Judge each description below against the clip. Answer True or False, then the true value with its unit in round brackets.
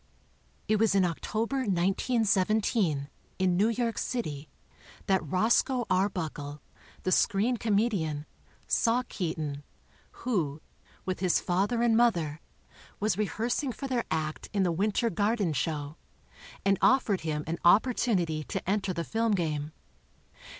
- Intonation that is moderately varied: False (5.7 semitones)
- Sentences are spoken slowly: True (130 wpm)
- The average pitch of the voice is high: True (195 Hz)